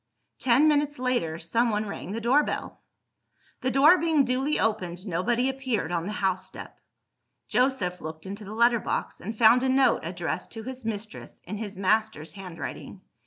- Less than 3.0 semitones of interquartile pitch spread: No, average, 5.1 semitones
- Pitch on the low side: No, high, 225 Hz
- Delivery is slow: No, average, 165 wpm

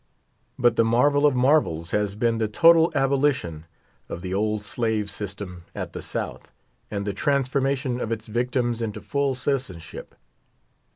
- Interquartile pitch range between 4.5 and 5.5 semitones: Yes, average, 4.8 semitones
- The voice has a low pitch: Yes, low, 115 Hz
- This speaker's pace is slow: No, average, 150 wpm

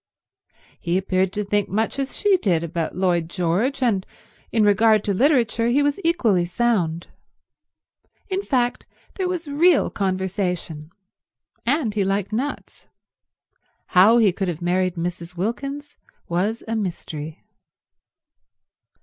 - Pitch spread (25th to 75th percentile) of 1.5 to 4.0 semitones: No, wide, 5.6 semitones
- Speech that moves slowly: Yes, slow, 125 wpm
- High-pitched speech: Yes, high, 205 Hz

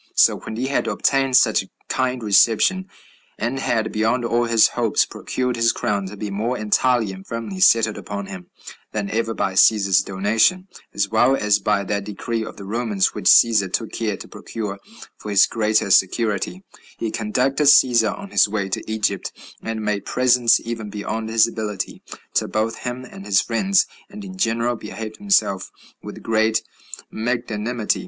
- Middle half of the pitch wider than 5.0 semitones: No, average, 2.7 semitones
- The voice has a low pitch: Yes, low, 110 Hz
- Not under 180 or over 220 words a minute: No, average, 170 wpm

